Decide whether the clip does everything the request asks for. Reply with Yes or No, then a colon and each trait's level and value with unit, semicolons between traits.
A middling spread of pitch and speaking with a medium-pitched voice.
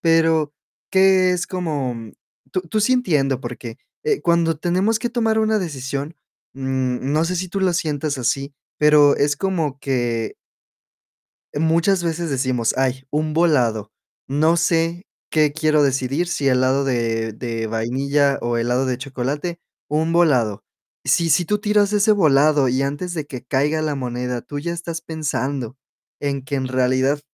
Yes: average, 4.6 semitones; medium, 145 Hz